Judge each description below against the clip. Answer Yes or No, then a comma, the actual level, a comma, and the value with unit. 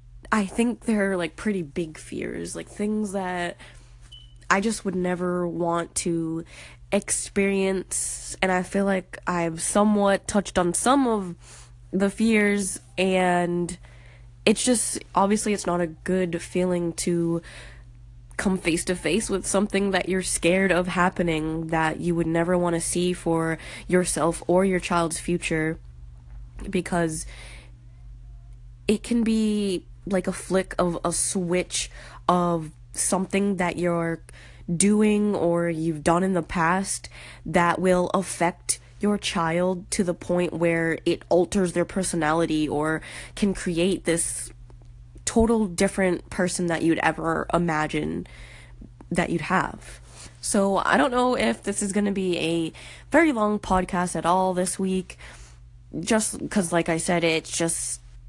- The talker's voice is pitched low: No, medium, 175 Hz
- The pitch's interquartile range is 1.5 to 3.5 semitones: Yes, average, 3.2 semitones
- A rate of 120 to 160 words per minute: Yes, average, 140 wpm